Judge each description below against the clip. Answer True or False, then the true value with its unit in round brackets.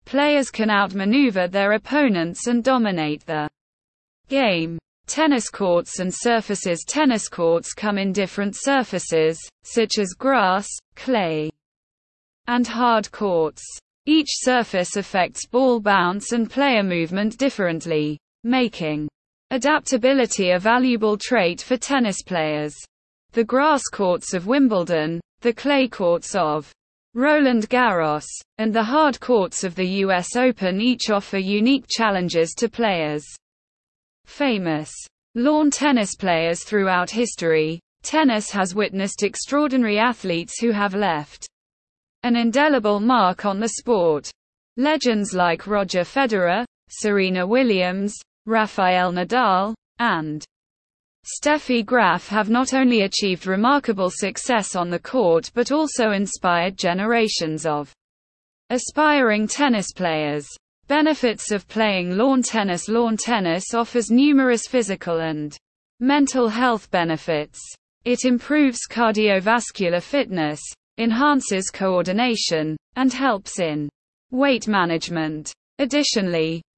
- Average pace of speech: False (110 wpm)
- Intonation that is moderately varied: False (5.8 semitones)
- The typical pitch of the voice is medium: False (210 Hz)